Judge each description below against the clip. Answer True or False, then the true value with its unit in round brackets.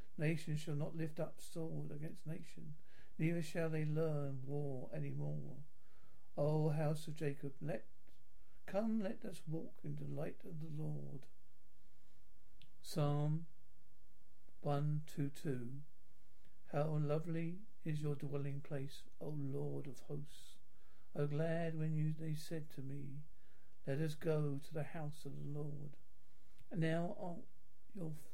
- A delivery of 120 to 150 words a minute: True (145 wpm)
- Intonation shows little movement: True (2.0 semitones)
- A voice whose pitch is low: False (150 Hz)